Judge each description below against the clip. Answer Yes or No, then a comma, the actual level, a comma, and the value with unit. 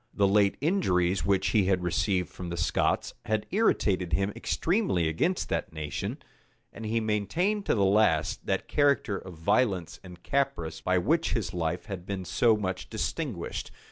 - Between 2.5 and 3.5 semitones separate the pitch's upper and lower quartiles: No, average, 4.3 semitones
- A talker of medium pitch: No, low, 100 Hz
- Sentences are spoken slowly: No, average, 165 wpm